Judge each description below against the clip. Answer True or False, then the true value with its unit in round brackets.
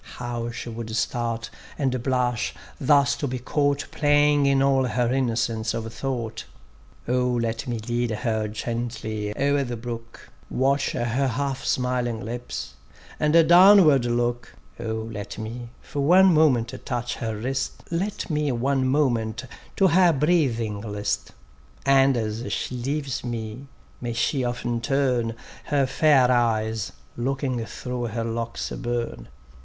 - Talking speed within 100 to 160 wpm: True (140 wpm)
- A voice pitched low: True (120 Hz)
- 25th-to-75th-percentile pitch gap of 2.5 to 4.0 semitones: True (3.2 semitones)